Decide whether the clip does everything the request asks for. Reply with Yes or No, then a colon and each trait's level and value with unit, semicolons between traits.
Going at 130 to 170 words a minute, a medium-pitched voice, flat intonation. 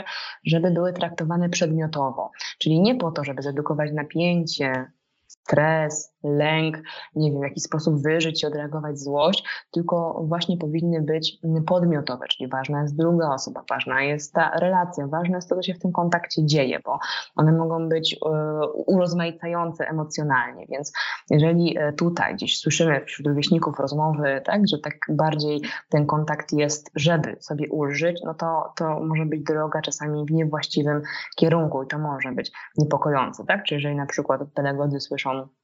Yes: average, 155 wpm; medium, 155 Hz; narrow, 2.0 semitones